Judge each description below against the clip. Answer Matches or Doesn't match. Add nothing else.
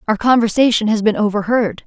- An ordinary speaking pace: Matches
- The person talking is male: Doesn't match